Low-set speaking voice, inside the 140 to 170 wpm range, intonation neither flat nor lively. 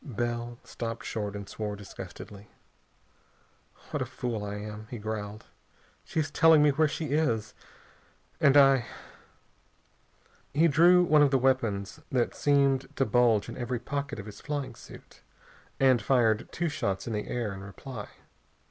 Yes: low, 120 Hz; average, 155 wpm; average, 5.0 semitones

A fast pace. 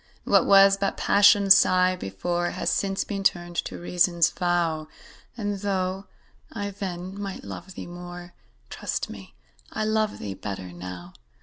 No: average, 145 wpm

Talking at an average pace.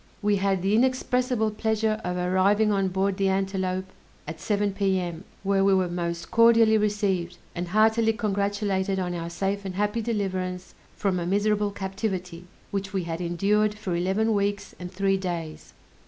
Yes: average, 160 wpm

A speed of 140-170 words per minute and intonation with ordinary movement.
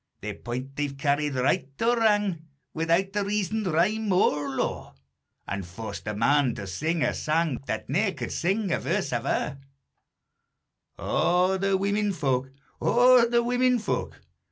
No: average, 150 wpm; wide, 7.0 semitones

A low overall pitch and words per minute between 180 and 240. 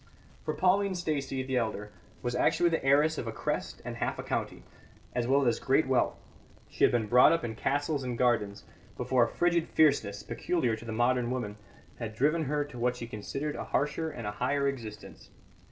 Yes: low, 130 Hz; average, 200 wpm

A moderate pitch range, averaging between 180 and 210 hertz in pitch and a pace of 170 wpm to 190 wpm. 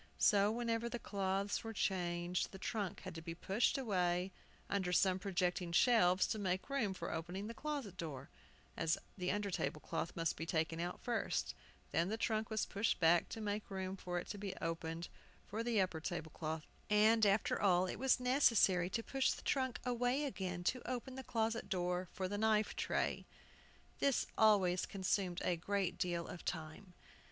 Yes: average, 4.0 semitones; high, 190 Hz; average, 180 wpm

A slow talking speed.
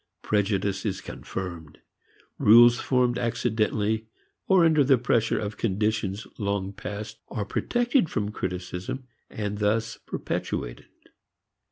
Yes: slow, 110 wpm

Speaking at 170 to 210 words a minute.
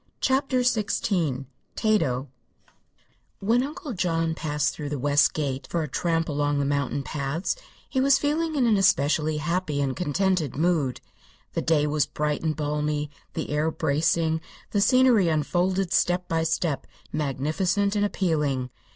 No: average, 145 wpm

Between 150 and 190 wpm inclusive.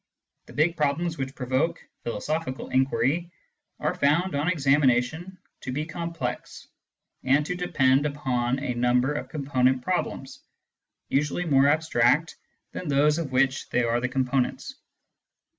No: slow, 135 wpm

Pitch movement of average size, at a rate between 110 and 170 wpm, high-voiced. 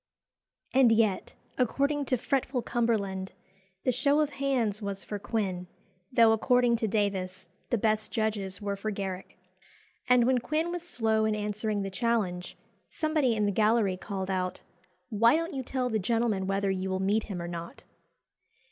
Yes: average, 4.1 semitones; average, 165 wpm; high, 220 Hz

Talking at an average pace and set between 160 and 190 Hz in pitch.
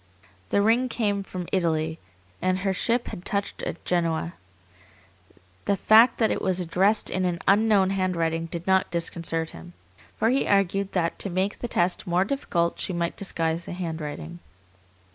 Yes: average, 160 wpm; medium, 185 Hz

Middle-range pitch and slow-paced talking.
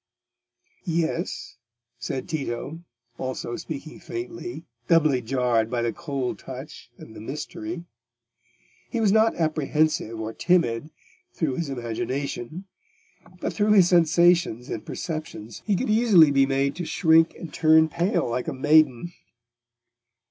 Yes: medium, 155 Hz; slow, 125 wpm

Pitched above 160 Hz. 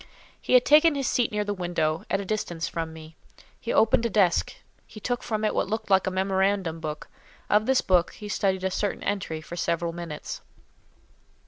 Yes: high, 190 Hz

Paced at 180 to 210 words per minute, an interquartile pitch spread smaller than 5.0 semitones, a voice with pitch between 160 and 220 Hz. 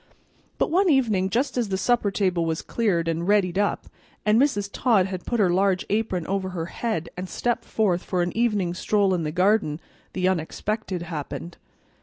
Yes: average, 185 wpm; average, 3.7 semitones; high, 190 Hz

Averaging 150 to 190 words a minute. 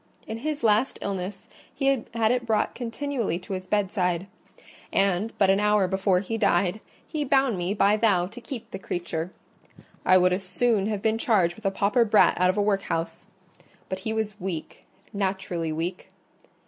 Yes: average, 175 wpm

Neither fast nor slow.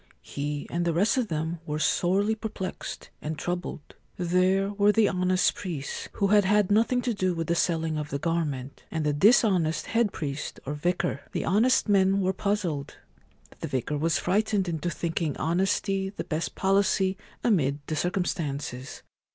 Yes: average, 165 wpm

